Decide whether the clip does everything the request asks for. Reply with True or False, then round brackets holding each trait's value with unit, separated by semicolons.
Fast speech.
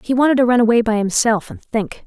True (260 wpm)